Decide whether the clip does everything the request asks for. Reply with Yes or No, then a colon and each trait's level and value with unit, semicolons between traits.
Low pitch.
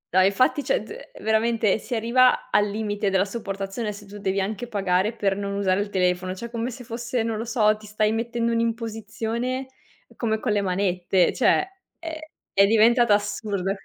No: high, 215 Hz